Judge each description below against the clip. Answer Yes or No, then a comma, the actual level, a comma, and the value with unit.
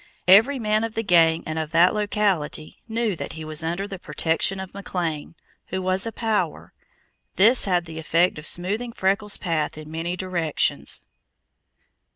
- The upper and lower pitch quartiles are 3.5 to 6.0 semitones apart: Yes, average, 4.3 semitones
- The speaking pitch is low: No, medium, 185 Hz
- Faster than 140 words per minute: Yes, average, 165 wpm